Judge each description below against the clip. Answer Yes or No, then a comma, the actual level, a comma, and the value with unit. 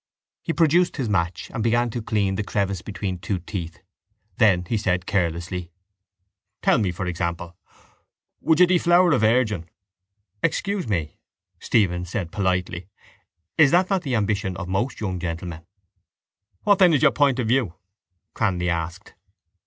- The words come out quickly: No, average, 150 wpm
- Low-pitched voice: Yes, low, 100 Hz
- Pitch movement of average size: No, wide, 6.1 semitones